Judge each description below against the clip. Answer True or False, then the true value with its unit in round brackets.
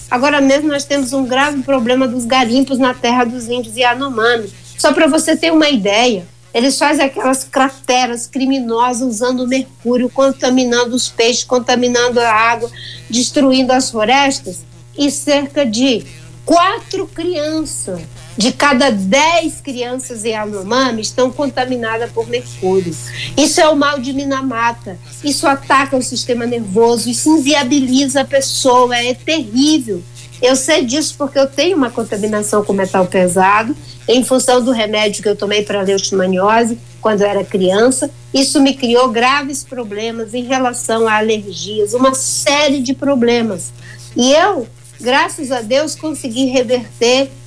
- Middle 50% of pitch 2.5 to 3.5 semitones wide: False (4.1 semitones)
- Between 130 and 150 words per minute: True (145 wpm)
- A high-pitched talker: True (250 Hz)